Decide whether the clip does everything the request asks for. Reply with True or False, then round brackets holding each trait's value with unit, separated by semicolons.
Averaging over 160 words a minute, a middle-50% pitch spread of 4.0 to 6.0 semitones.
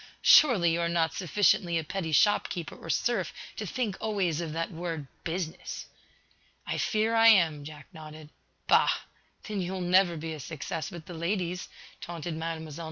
False (170 wpm; 3.1 semitones)